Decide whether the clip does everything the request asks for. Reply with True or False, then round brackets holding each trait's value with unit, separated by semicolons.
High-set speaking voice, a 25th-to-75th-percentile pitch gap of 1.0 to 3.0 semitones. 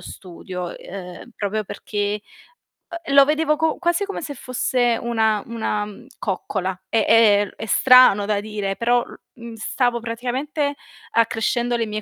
False (230 Hz; 3.5 semitones)